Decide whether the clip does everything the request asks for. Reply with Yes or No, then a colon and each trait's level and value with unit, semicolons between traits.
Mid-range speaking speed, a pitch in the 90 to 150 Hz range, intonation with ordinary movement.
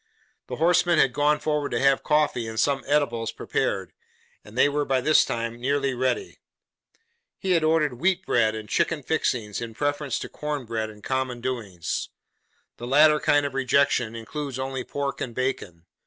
Yes: average, 170 wpm; low, 135 Hz; average, 4.0 semitones